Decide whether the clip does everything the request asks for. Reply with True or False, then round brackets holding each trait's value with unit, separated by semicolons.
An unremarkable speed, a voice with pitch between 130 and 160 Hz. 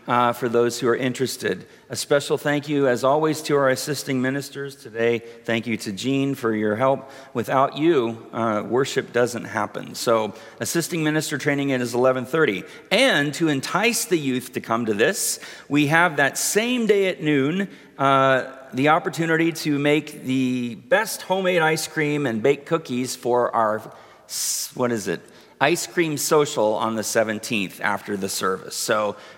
True (165 wpm; 135 Hz)